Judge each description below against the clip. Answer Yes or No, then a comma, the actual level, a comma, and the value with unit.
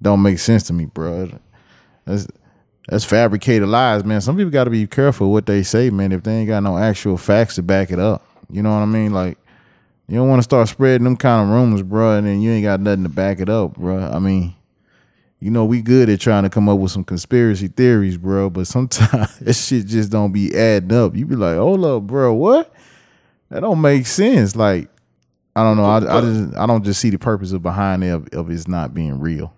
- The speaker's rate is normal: No, fast, 235 wpm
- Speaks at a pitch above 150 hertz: No, low, 105 Hz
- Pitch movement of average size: Yes, average, 3.4 semitones